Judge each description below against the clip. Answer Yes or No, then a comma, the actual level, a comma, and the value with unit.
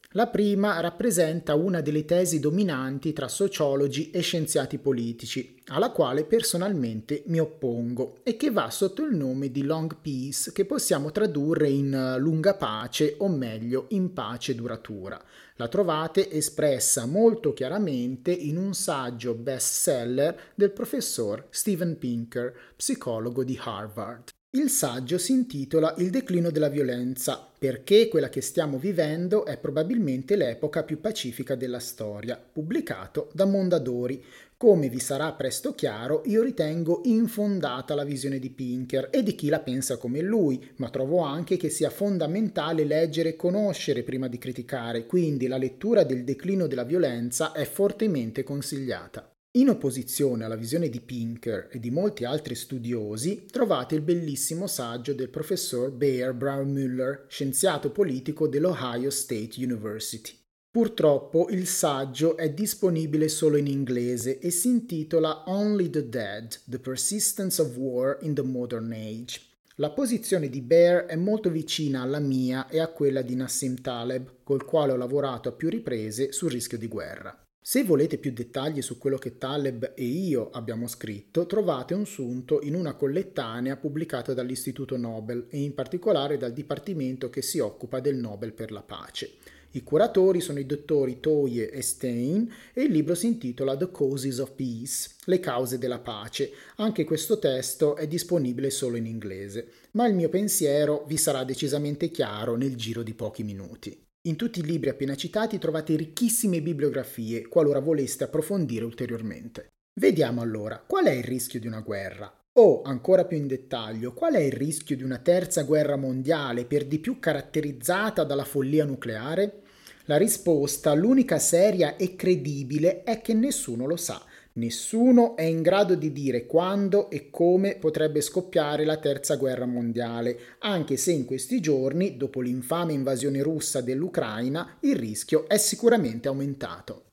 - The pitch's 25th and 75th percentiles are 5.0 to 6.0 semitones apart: Yes, average, 5.3 semitones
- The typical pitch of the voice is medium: Yes, medium, 145 Hz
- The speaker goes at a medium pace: Yes, average, 155 wpm